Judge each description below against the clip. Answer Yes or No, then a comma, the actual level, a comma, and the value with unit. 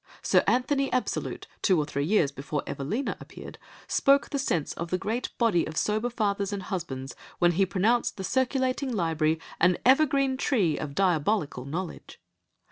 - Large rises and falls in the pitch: Yes, wide, 7.6 semitones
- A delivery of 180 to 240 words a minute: No, average, 160 wpm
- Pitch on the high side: Yes, high, 195 Hz